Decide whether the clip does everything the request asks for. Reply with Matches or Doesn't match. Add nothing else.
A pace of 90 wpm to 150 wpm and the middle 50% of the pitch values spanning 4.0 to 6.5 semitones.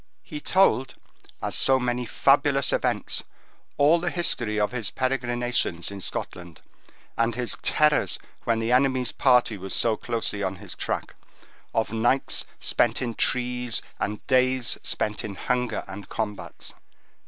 Doesn't match